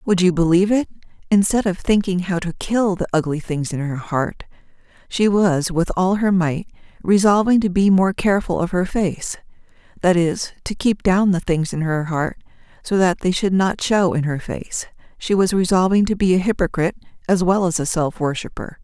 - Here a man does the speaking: No, female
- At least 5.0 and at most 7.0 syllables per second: Yes, 5.1 syllables/s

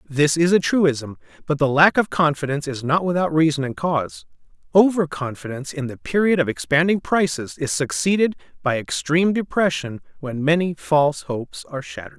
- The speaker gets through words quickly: No, average, 165 wpm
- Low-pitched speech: No, medium, 150 Hz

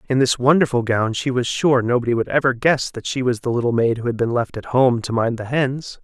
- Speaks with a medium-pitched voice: No, low, 125 Hz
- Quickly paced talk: Yes, fast, 270 wpm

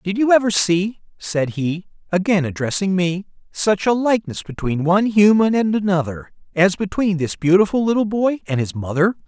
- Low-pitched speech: No, high, 190 Hz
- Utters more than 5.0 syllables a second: Yes, 5.2 syllables/s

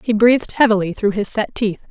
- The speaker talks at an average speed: No, fast, 220 wpm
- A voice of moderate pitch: No, high, 215 Hz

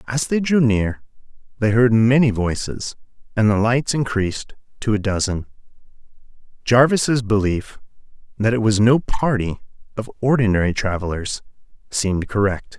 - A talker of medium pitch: No, low, 115 Hz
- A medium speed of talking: No, slow, 125 wpm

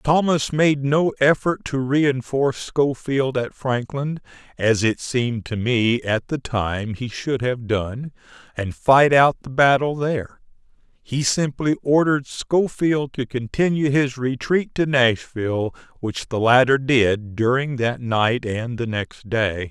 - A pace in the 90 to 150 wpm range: Yes, average, 145 wpm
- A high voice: No, low, 130 Hz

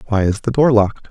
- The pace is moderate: No, fast, 270 wpm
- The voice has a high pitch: No, low, 110 Hz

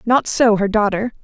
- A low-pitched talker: No, high, 220 Hz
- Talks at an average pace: Yes, average, 195 wpm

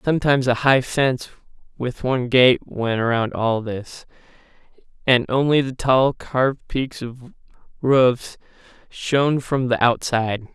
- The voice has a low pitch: Yes, low, 125 Hz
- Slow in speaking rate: Yes, slow, 130 wpm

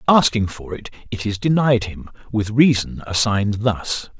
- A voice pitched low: Yes, low, 110 Hz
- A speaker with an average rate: Yes, average, 155 wpm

